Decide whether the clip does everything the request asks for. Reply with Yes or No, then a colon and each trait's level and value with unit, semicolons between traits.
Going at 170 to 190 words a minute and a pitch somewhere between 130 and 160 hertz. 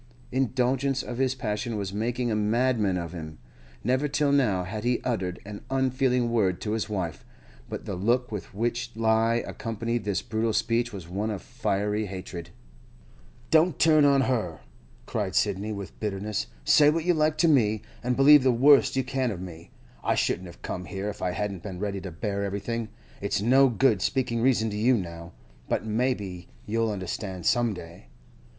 No: average, 180 wpm; low, 110 Hz